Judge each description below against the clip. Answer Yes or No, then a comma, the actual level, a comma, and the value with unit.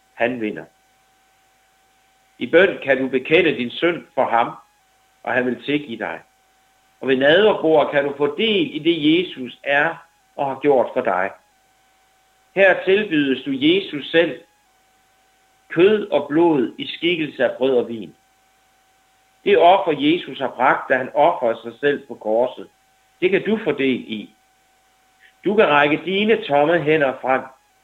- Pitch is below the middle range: No, medium, 155 Hz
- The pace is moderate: Yes, average, 155 wpm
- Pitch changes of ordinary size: No, wide, 8.8 semitones